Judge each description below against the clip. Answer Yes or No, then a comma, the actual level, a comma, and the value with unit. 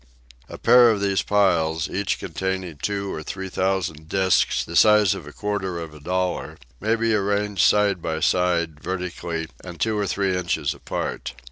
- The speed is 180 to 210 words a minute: No, average, 170 wpm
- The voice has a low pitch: Yes, very low, 95 Hz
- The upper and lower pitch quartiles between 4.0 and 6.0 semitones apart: No, average, 3.2 semitones